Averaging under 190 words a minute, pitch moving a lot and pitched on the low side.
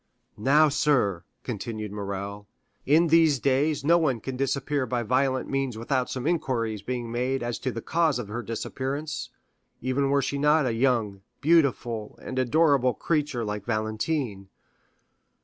No: average, 150 wpm; average, 4.0 semitones; low, 130 Hz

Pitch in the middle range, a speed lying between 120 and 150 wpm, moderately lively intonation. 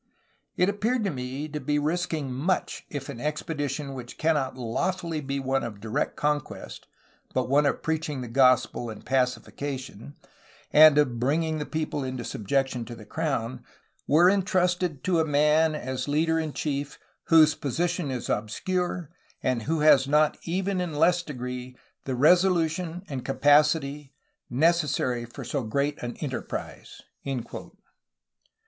Yes: medium, 145 Hz; average, 140 wpm; average, 3.9 semitones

